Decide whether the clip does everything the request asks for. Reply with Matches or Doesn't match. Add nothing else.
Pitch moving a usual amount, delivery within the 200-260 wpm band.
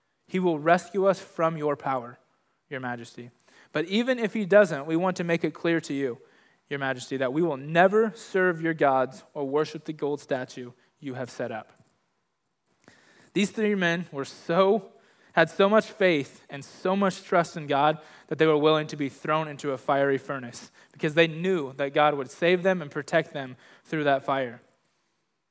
Doesn't match